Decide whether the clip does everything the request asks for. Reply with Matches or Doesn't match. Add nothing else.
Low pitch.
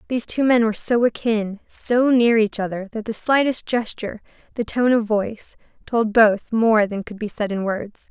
Doesn't match